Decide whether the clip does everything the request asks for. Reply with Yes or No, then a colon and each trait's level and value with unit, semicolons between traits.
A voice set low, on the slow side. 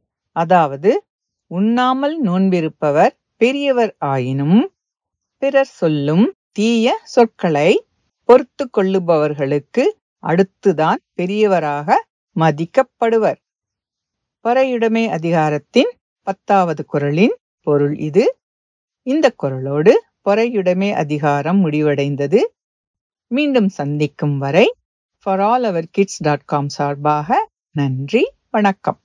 No: high, 195 Hz; slow, 75 wpm